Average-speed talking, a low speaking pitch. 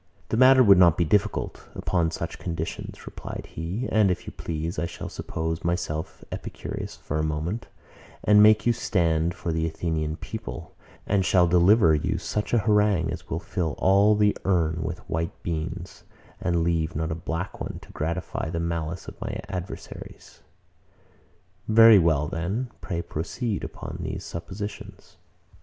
Yes: average, 155 wpm; very low, 85 Hz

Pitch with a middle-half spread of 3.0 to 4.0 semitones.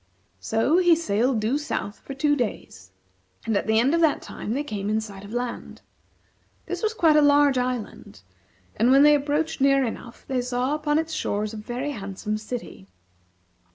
No: average, 5.2 semitones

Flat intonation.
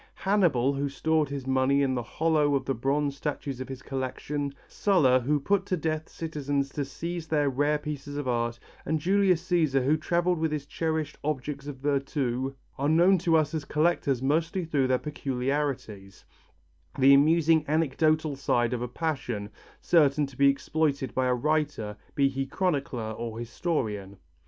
No: average, 3.1 semitones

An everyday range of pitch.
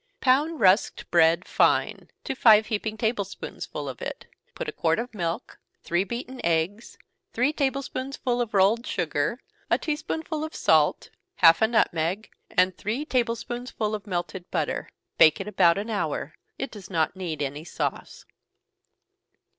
No: wide, 6.1 semitones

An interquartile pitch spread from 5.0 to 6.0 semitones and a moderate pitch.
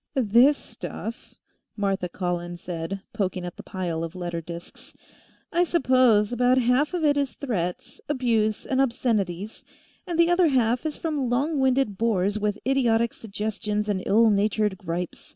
No: wide, 5.5 semitones; high, 220 Hz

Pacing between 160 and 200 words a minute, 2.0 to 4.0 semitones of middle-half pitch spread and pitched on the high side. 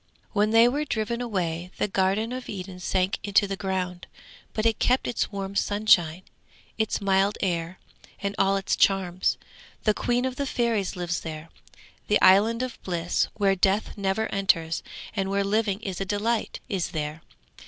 Yes: average, 165 wpm; average, 2.9 semitones; high, 195 Hz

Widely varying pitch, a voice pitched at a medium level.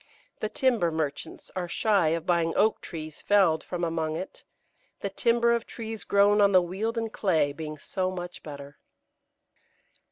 No: average, 4.8 semitones; medium, 180 Hz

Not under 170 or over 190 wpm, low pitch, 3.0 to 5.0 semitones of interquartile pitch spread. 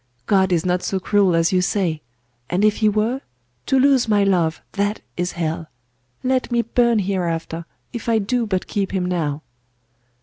No: average, 175 wpm; high, 195 Hz; average, 4.0 semitones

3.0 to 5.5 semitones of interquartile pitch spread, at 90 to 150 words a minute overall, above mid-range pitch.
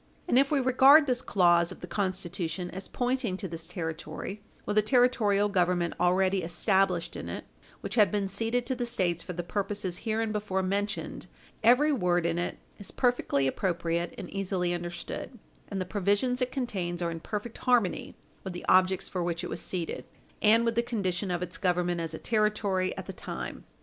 No: average, 4.1 semitones; average, 185 wpm; high, 195 Hz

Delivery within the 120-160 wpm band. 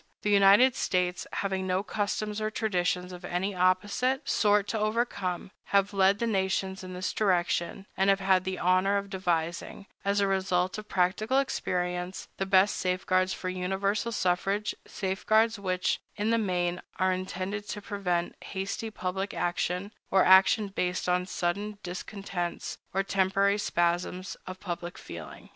Yes: average, 150 wpm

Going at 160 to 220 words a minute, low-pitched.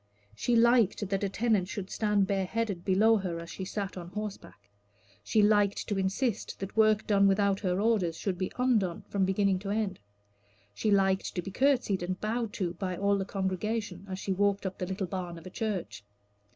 No: average, 195 wpm; high, 195 Hz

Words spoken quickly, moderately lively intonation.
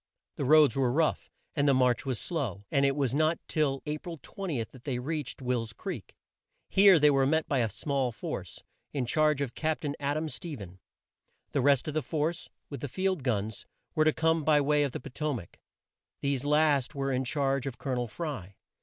Yes: fast, 215 wpm; average, 3.4 semitones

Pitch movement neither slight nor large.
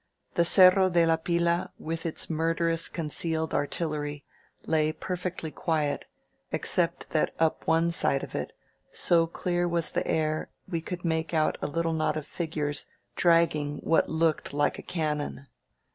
No: narrow, 1.7 semitones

